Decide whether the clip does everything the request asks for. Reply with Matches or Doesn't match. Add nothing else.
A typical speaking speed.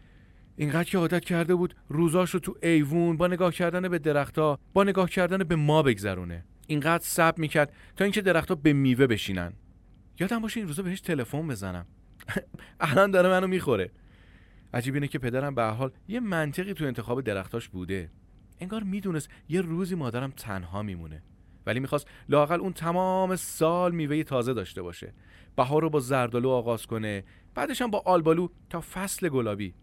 Doesn't match